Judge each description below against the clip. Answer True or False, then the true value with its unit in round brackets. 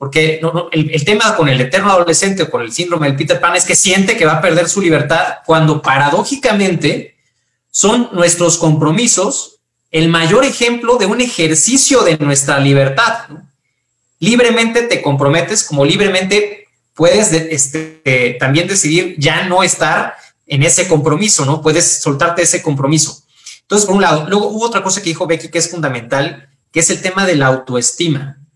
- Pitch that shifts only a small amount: False (4.6 semitones)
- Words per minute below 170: False (175 wpm)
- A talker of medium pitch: True (165 Hz)